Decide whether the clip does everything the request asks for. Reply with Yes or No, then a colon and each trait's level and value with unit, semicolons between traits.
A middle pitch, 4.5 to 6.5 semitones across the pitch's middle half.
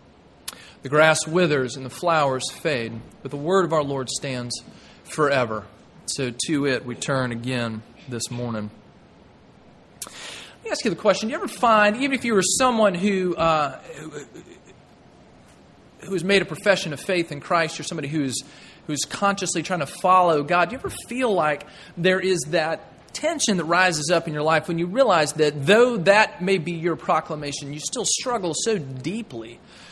Yes: medium, 165 Hz; average, 5.3 semitones